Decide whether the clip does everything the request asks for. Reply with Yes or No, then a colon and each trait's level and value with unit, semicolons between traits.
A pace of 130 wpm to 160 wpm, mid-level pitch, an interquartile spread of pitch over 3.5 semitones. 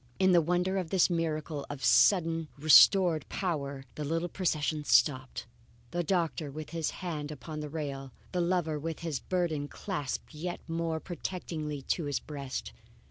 No: average, 155 wpm; medium, 160 Hz; average, 2.9 semitones